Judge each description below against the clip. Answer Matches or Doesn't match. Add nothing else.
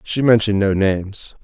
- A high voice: Doesn't match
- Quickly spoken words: Doesn't match